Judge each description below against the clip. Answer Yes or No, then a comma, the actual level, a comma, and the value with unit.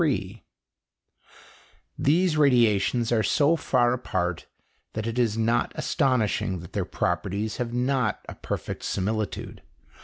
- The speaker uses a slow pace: Yes, slow, 120 wpm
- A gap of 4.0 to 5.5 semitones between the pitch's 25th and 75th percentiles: No, average, 3.3 semitones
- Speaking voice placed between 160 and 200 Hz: No, low, 115 Hz